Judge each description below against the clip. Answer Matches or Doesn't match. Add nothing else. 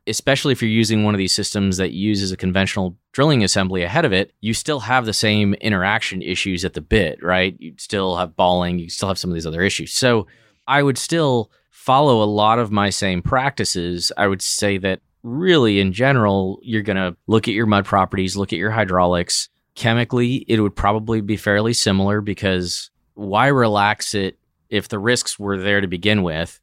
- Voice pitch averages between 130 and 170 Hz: Doesn't match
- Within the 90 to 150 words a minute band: Doesn't match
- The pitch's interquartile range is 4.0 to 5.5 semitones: Doesn't match